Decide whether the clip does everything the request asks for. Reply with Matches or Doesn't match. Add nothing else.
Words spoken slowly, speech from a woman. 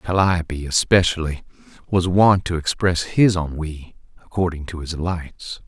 Doesn't match